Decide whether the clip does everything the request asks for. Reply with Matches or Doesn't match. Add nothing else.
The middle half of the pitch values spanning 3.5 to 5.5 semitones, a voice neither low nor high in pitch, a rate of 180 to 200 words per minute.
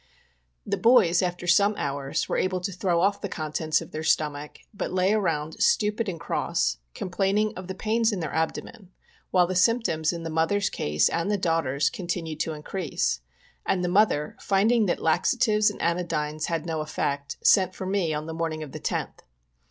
Matches